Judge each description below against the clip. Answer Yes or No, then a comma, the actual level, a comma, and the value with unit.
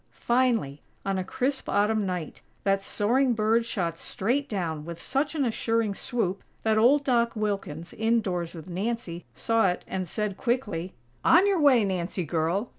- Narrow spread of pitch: No, average, 4.8 semitones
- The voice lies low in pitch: No, high, 210 Hz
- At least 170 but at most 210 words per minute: No, average, 160 wpm